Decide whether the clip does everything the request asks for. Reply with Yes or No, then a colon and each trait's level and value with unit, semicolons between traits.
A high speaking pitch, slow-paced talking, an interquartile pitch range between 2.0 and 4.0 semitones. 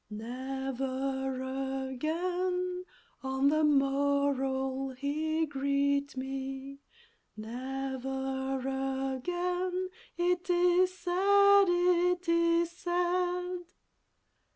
No: very high, 280 Hz; slow, 65 wpm; average, 4.9 semitones